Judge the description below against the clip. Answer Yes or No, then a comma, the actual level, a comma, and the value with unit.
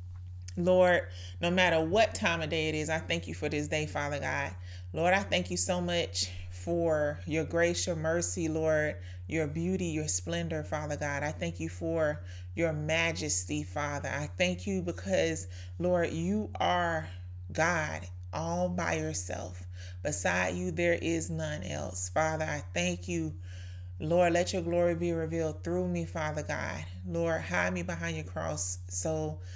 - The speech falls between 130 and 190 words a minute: Yes, average, 160 wpm